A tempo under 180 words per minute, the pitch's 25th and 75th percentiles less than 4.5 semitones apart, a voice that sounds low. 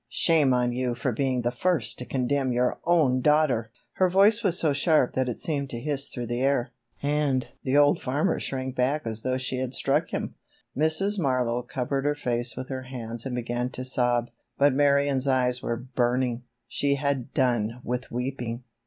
No: average, 185 wpm; narrow, 2.5 semitones; low, 130 Hz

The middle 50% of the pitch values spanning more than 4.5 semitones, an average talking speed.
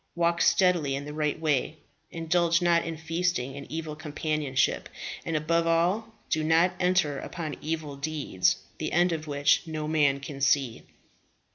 No: narrow, 2.6 semitones; average, 155 wpm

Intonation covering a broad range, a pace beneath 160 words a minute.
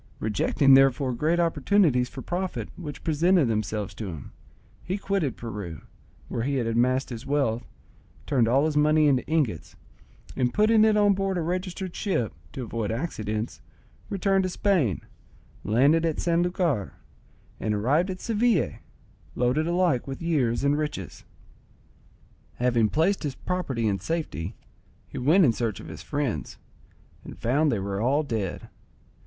Yes: wide, 6.9 semitones; average, 150 wpm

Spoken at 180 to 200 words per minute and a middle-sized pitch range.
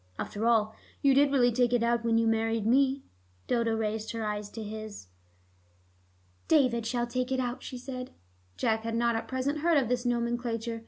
No: average, 190 wpm; narrow, 2.1 semitones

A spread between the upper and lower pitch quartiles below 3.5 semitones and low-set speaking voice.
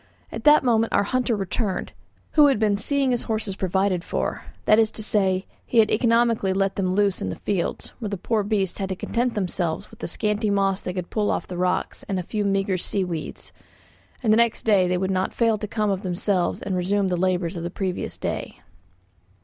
No: average, 2.9 semitones; high, 200 Hz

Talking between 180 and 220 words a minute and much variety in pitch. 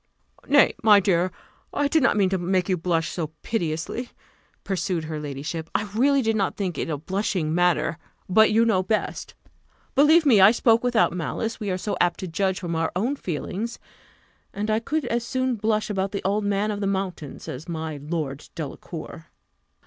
No: average, 190 wpm; average, 4.8 semitones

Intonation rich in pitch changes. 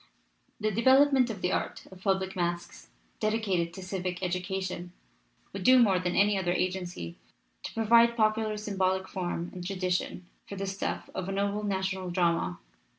No: average, 2.8 semitones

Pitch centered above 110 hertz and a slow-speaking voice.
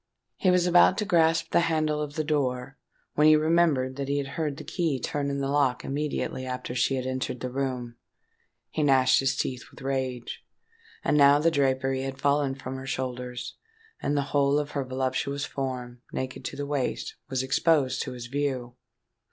No: low, 135 Hz; average, 190 wpm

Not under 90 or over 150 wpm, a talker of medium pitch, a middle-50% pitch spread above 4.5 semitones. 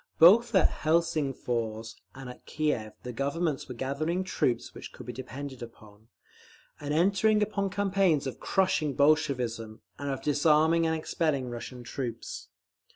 Yes: average, 140 wpm; medium, 145 Hz; average, 5.1 semitones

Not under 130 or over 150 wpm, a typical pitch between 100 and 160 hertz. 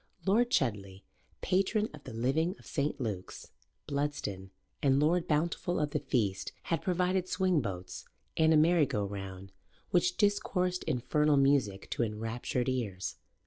Yes: average, 145 wpm; medium, 140 Hz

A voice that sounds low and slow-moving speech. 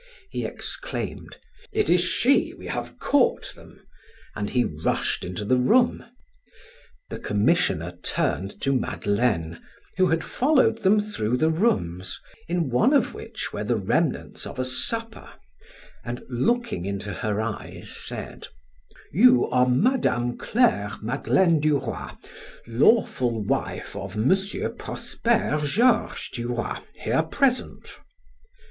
Yes: low, 130 Hz; slow, 125 wpm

